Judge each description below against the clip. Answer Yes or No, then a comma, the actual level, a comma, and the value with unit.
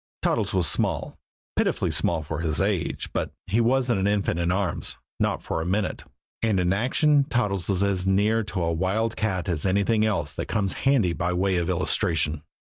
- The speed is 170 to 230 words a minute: Yes, average, 190 wpm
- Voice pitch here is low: Yes, very low, 95 Hz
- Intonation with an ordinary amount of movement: Yes, average, 3.6 semitones